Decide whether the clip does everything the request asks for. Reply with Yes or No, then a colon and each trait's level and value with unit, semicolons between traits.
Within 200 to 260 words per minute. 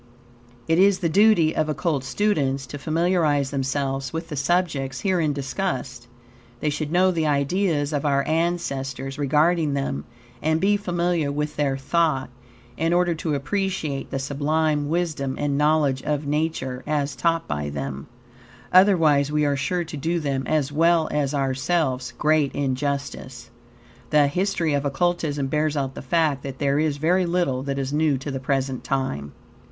No: average, 160 wpm